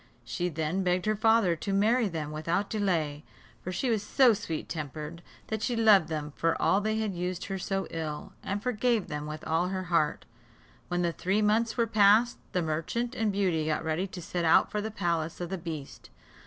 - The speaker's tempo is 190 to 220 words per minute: Yes, fast, 205 wpm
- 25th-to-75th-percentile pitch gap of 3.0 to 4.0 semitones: No, average, 4.8 semitones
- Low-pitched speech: No, medium, 185 Hz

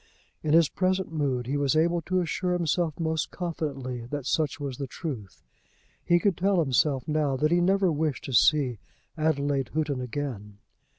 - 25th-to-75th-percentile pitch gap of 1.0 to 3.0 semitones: No, average, 4.0 semitones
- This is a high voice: No, medium, 150 Hz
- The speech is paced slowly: No, average, 170 wpm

